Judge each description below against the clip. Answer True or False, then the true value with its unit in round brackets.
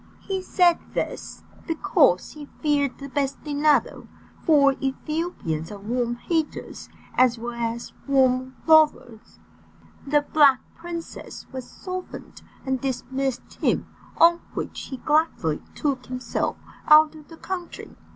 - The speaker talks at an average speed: False (120 wpm)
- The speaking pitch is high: True (280 Hz)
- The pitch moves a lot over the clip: False (3.8 semitones)